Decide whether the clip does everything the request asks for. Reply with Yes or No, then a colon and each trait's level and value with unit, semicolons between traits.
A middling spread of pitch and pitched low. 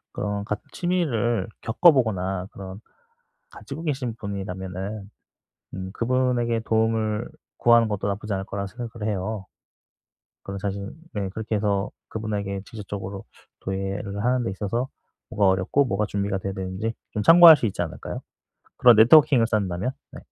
Yes: average, 3.2 semitones; low, 105 Hz